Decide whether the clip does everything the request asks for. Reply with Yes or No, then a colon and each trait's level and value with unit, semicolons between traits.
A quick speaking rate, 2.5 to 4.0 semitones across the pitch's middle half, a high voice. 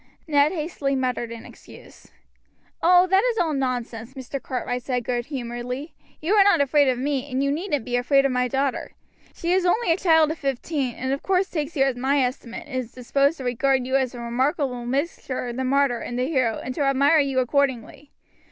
Yes: fast, 210 wpm; average, 3.0 semitones; very high, 270 Hz